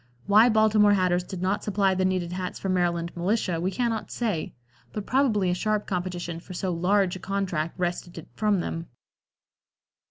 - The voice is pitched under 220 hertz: Yes, medium, 185 Hz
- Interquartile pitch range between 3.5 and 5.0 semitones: No, average, 2.8 semitones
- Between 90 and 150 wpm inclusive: No, average, 170 wpm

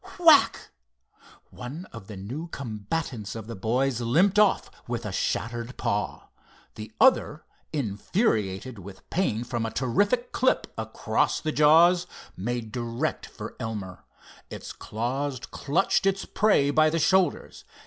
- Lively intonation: Yes, wide, 6.9 semitones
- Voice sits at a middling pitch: No, low, 125 Hz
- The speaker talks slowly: Yes, slow, 130 wpm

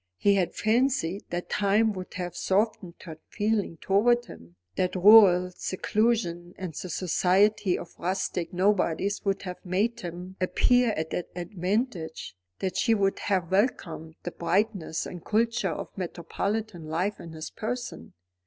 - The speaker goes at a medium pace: Yes, average, 145 wpm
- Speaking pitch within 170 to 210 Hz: Yes, high, 190 Hz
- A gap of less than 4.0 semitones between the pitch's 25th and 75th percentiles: Yes, average, 3.4 semitones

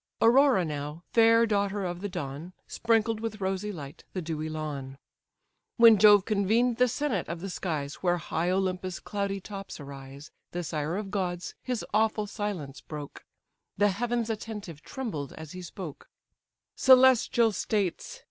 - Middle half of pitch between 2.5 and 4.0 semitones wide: No, average, 5.3 semitones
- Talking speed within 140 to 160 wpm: Yes, average, 150 wpm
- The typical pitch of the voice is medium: No, high, 195 Hz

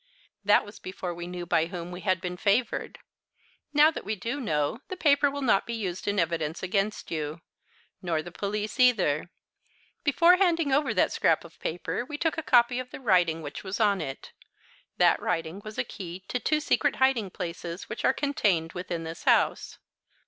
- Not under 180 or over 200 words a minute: Yes, average, 190 wpm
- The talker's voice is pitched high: Yes, high, 200 Hz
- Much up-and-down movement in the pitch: Yes, wide, 6.6 semitones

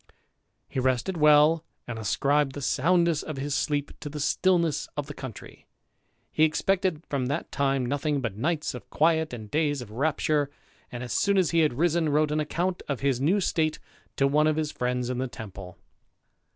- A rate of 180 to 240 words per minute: Yes, average, 190 wpm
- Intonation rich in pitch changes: No, average, 3.4 semitones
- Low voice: No, medium, 145 Hz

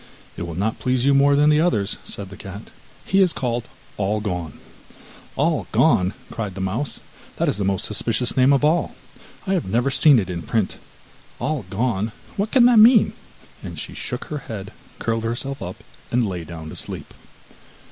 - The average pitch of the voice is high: No, low, 115 Hz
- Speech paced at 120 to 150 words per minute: No, average, 190 wpm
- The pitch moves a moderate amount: No, wide, 6.4 semitones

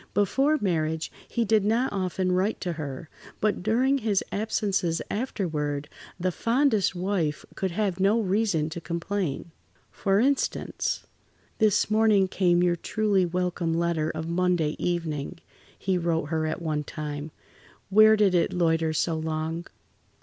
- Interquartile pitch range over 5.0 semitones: No, average, 4.2 semitones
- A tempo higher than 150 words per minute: No, average, 140 wpm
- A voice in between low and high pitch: Yes, medium, 180 Hz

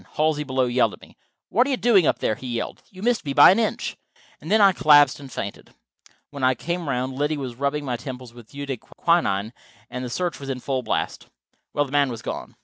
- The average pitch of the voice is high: No, medium, 140 Hz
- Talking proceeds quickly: Yes, fast, 235 wpm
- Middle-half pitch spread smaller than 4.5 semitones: Yes, average, 3.8 semitones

